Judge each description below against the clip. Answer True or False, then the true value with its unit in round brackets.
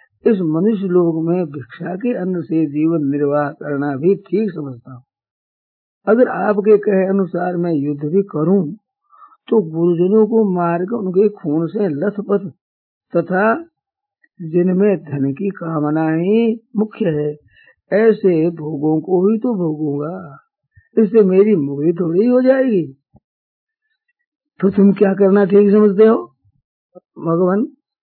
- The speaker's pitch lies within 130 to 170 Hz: False (185 Hz)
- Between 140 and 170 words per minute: False (125 wpm)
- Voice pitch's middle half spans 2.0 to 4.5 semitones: False (5.5 semitones)